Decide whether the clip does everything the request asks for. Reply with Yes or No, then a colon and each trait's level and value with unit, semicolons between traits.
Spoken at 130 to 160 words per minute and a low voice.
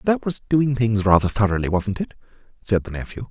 No: average, 200 wpm; low, 110 Hz